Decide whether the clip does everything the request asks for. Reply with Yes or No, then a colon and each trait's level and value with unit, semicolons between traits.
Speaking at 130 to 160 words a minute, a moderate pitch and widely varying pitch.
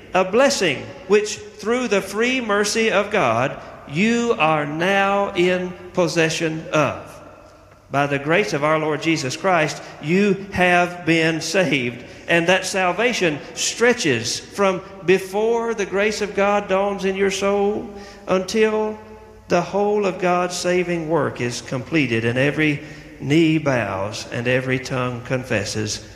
Yes: slow, 135 wpm; medium, 180 Hz; wide, 5.8 semitones